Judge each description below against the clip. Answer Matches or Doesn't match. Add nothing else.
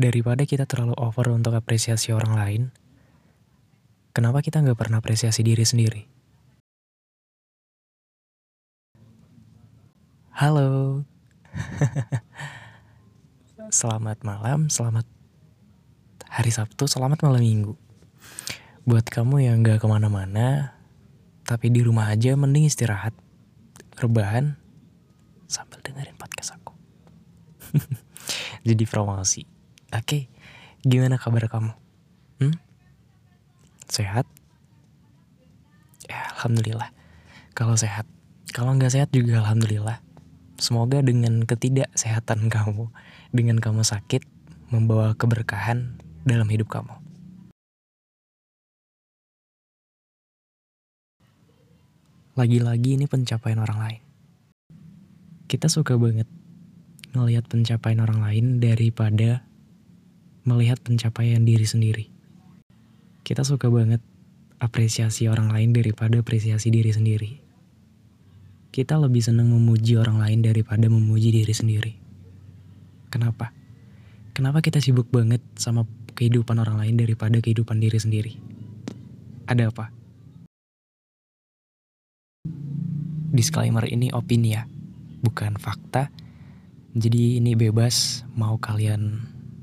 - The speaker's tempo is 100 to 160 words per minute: Doesn't match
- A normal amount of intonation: Matches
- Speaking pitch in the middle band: Doesn't match